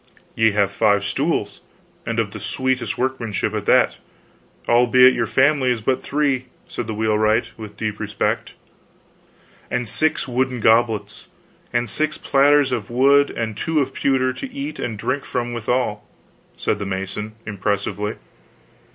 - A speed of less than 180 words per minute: Yes, average, 145 wpm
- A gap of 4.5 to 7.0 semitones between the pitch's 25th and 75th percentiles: No, average, 3.6 semitones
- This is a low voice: Yes, low, 120 Hz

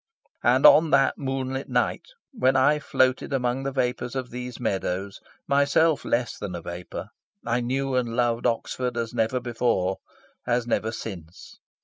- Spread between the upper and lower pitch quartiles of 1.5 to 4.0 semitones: Yes, narrow, 2.6 semitones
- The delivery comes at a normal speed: Yes, average, 150 wpm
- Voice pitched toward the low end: Yes, low, 125 Hz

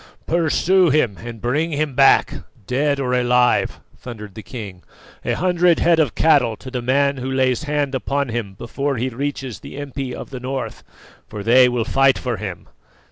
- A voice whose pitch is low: Yes, low, 130 Hz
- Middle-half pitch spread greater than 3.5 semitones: No, average, 3.2 semitones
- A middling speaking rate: Yes, average, 180 wpm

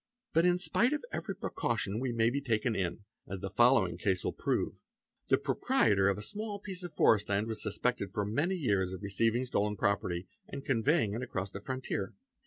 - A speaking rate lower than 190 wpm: No, fast, 205 wpm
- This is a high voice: No, low, 110 Hz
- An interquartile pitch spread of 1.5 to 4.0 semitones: No, average, 5.2 semitones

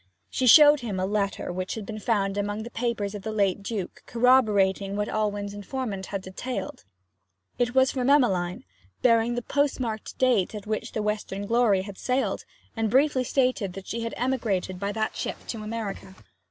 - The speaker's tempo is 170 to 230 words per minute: Yes, average, 175 wpm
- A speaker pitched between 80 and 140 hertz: No, high, 215 Hz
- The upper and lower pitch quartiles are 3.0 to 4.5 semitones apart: Yes, average, 3.6 semitones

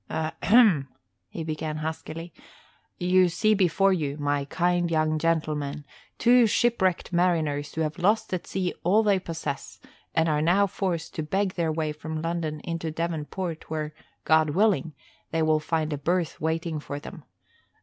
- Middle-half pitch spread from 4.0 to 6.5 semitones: No, average, 2.9 semitones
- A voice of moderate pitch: Yes, medium, 165 Hz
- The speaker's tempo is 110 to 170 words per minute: Yes, average, 160 wpm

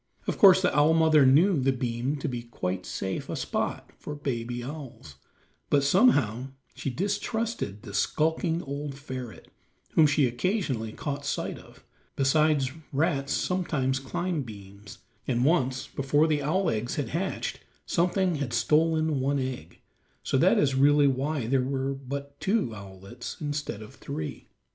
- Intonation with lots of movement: No, average, 4.3 semitones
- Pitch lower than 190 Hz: Yes, medium, 140 Hz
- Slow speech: No, average, 150 wpm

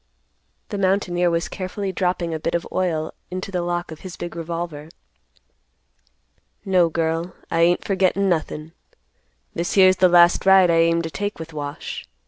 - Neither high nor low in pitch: Yes, medium, 175 Hz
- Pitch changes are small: Yes, narrow, 2.0 semitones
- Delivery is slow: No, average, 160 wpm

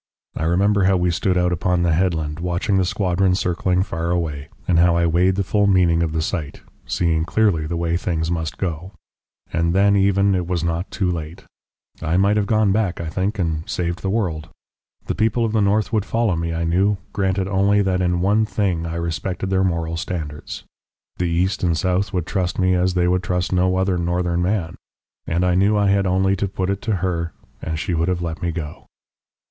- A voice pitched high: No, very low, 90 Hz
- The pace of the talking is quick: Yes, fast, 215 wpm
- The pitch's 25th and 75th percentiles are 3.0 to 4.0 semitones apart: No, narrow, 2.4 semitones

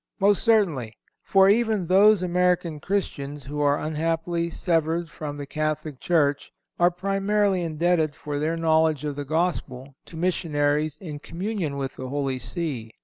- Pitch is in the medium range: Yes, medium, 160 Hz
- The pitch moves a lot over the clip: No, average, 3.7 semitones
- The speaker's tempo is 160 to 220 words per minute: No, average, 145 wpm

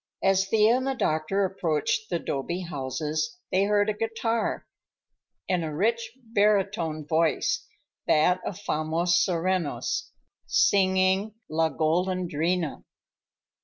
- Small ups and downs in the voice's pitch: No, average, 4.4 semitones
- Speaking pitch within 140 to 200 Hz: Yes, medium, 185 Hz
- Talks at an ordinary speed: No, slow, 100 wpm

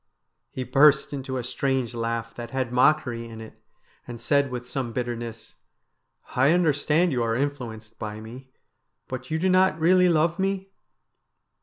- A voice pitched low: Yes, low, 130 Hz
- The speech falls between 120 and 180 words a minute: Yes, average, 160 wpm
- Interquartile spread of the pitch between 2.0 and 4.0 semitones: No, average, 4.6 semitones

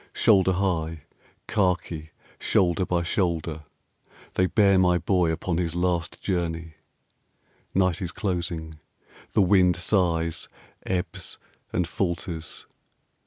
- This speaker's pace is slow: Yes, slow, 105 wpm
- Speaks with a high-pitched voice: No, very low, 90 Hz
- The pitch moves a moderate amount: No, narrow, 2.1 semitones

